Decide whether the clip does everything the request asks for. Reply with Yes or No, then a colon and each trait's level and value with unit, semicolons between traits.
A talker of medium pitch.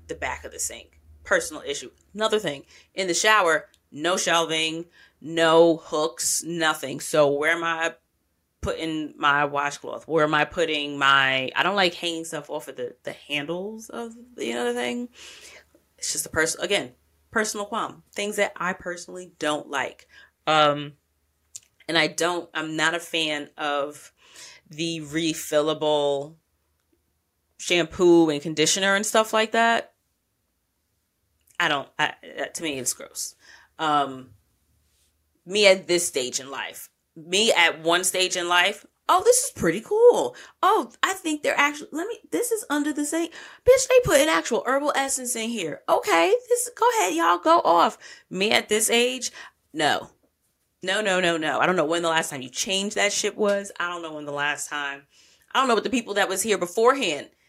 Yes: medium, 165 Hz